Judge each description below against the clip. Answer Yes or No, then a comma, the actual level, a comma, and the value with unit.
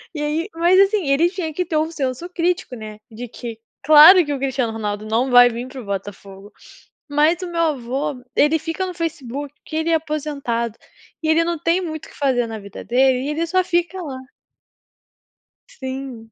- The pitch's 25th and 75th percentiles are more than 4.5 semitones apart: Yes, average, 5.3 semitones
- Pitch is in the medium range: No, very high, 290 Hz